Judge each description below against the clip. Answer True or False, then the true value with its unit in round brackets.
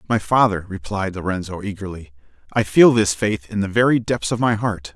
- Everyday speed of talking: True (195 wpm)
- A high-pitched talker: False (105 Hz)